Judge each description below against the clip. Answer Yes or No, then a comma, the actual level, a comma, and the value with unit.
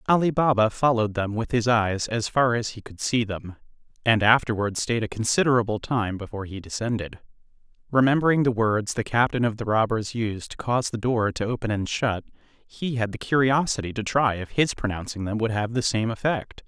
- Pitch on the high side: No, low, 115 Hz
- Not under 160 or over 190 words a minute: No, average, 200 wpm